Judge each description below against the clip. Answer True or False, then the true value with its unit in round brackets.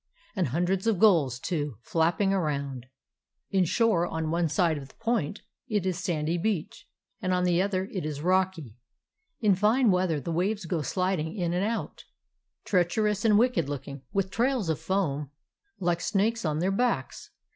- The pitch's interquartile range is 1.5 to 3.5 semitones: False (4.0 semitones)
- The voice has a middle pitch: True (180 Hz)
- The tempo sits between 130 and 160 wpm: False (175 wpm)